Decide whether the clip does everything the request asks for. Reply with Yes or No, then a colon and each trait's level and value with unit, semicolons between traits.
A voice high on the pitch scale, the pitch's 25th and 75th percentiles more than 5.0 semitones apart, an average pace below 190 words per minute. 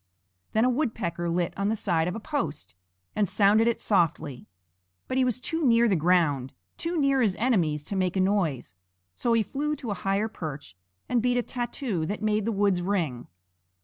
No: high, 205 Hz; wide, 5.6 semitones; average, 195 wpm